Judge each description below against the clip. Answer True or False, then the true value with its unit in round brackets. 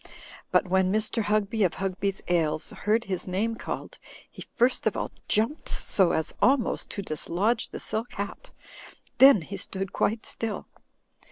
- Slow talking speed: False (155 wpm)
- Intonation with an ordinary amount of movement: True (3.2 semitones)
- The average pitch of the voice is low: False (205 Hz)